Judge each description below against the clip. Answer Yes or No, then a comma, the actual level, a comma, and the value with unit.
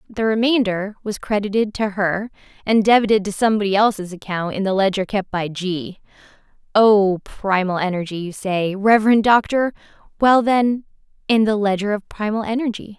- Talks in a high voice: Yes, high, 205 Hz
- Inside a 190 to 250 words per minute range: No, average, 150 wpm